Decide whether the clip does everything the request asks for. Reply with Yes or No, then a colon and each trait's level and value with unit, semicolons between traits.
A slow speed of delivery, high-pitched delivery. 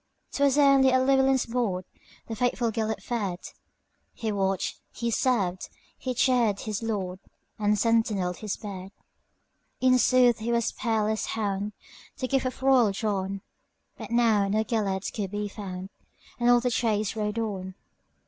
Yes: slow, 130 wpm; high, 220 Hz